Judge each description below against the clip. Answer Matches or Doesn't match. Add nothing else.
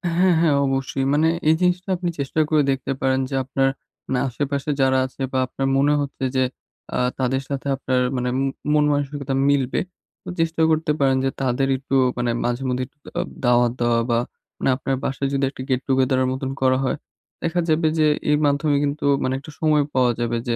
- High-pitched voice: Doesn't match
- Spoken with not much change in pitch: Matches